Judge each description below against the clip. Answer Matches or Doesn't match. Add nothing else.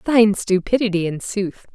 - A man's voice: Doesn't match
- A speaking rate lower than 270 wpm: Matches